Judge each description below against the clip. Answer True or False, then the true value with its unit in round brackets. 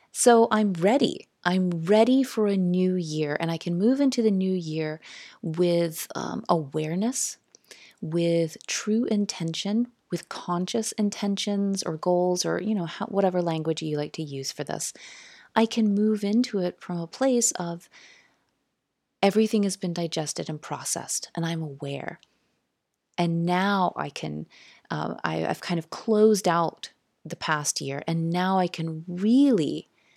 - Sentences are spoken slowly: False (155 wpm)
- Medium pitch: True (180 Hz)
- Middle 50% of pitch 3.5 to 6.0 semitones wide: True (4.7 semitones)